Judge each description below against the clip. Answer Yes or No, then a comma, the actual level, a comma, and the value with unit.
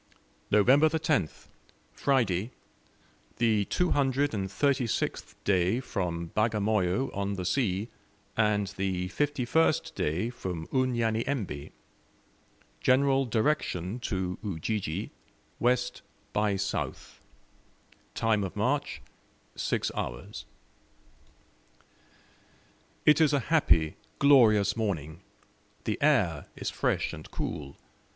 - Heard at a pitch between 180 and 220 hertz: No, low, 110 Hz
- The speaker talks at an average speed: No, slow, 85 wpm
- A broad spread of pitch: Yes, wide, 5.8 semitones